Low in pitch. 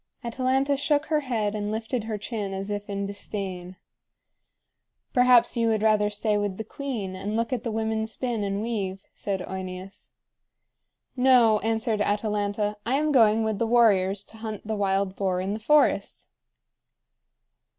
No: high, 215 Hz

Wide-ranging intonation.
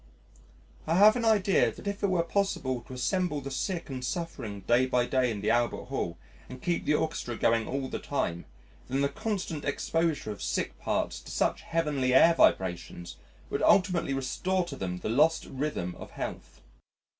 Yes: wide, 6.0 semitones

